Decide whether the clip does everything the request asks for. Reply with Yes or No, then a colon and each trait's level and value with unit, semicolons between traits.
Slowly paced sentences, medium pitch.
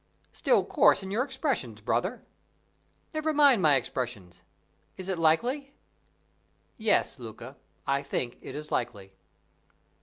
Yes: slow, 120 wpm; medium, 155 Hz